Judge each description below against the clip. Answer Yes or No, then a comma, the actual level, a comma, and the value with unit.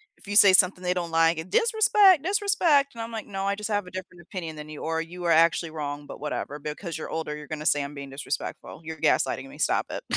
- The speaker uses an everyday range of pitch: Yes, average, 4.9 semitones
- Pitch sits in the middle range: Yes, medium, 170 Hz